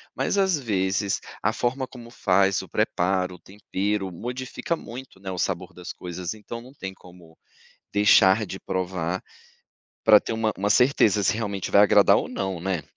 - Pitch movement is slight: No, average, 3.5 semitones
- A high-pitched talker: No, low, 100 Hz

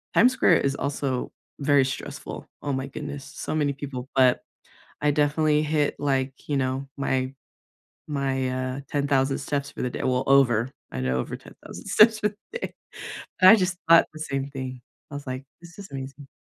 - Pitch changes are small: Yes, narrow, 2.1 semitones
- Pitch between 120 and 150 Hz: Yes, medium, 140 Hz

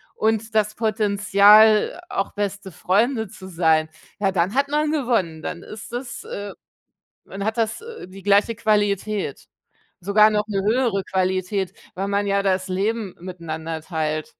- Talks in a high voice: Yes, high, 200 Hz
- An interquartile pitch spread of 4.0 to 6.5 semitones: No, average, 2.7 semitones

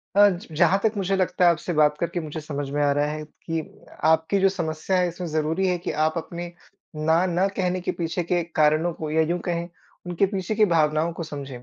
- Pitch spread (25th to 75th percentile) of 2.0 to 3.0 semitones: Yes, average, 2.7 semitones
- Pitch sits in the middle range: Yes, medium, 170 Hz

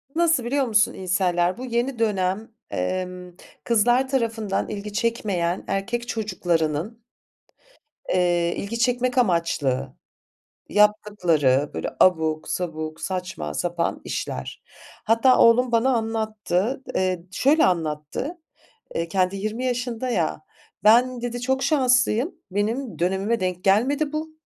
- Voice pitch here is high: Yes, high, 210 Hz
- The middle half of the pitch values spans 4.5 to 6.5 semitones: Yes, average, 5.3 semitones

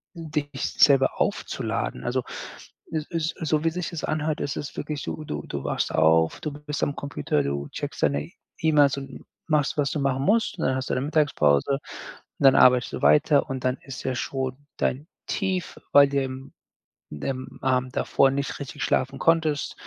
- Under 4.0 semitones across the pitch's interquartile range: Yes, average, 2.8 semitones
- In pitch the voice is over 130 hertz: Yes, medium, 140 Hz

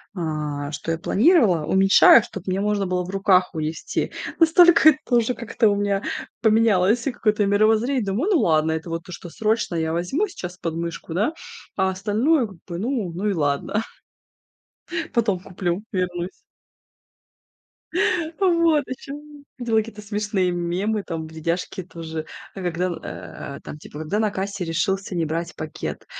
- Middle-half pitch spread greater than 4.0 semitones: Yes, average, 4.6 semitones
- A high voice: Yes, high, 195 Hz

